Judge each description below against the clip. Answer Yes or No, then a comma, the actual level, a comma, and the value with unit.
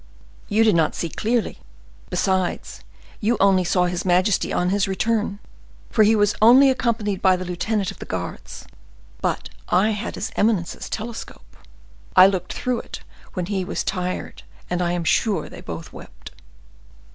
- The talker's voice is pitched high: Yes, high, 195 Hz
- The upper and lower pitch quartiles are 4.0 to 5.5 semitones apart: No, average, 3.3 semitones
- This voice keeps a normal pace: Yes, average, 160 wpm